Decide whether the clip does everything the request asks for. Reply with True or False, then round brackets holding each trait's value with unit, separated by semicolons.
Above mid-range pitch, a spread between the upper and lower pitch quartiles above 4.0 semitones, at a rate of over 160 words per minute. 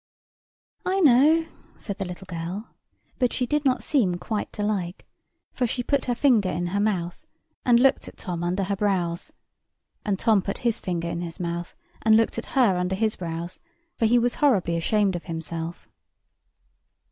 True (200 Hz; 5.4 semitones; 180 wpm)